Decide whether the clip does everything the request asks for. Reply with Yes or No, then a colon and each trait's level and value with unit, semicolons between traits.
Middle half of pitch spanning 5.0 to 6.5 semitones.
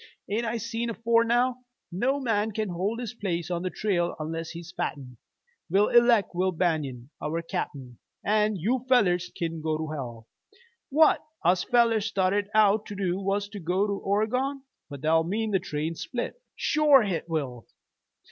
Yes: wide, 5.5 semitones